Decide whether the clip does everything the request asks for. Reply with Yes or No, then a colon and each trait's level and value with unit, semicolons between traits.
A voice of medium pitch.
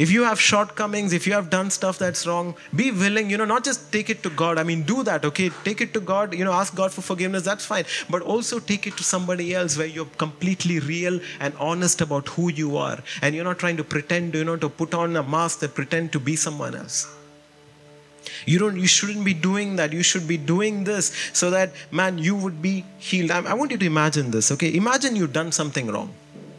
Yes: medium, 180 Hz